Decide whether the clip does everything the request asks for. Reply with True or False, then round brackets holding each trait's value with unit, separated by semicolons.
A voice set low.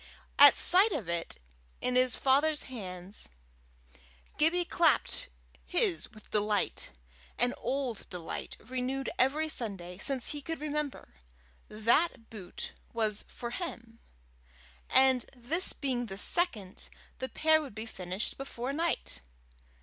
False (250 Hz)